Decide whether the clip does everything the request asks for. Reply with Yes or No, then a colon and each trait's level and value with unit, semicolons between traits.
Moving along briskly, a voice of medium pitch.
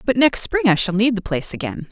No: fast, 280 wpm; high, 215 Hz